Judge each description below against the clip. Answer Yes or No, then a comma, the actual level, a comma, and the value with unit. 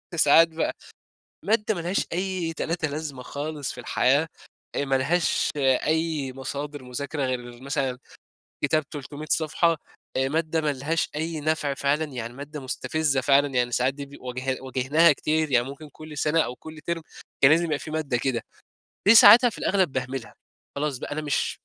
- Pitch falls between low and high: Yes, medium, 145 Hz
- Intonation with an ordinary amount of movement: Yes, average, 3.1 semitones